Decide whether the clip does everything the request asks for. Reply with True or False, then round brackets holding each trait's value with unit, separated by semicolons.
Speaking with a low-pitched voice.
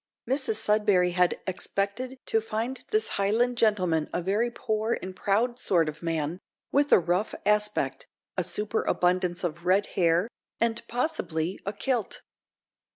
False (200 Hz)